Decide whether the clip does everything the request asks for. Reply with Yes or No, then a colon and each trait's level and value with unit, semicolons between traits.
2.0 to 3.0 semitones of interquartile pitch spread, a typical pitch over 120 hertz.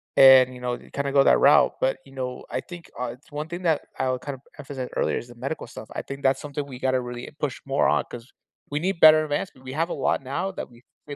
Yes: narrow, 2.6 semitones; low, 135 Hz